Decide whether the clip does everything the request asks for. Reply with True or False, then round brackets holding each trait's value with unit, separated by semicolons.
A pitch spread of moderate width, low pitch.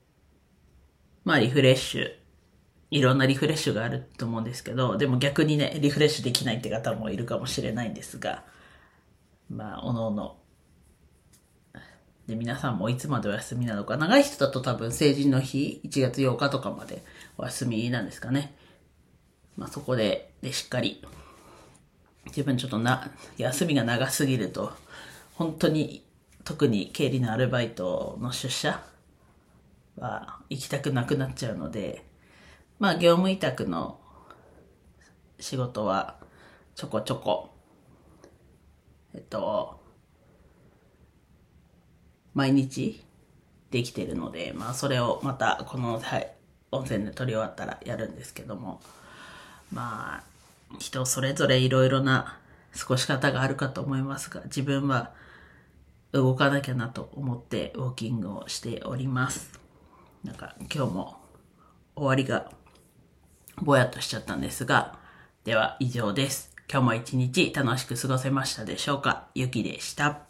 True (4.0 semitones; 130 Hz)